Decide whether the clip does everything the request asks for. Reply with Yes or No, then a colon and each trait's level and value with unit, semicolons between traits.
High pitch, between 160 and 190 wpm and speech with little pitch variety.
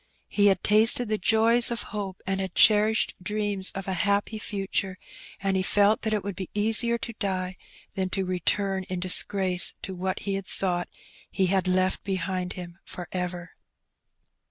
Yes: high, 195 Hz; average, 175 wpm; narrow, 2.1 semitones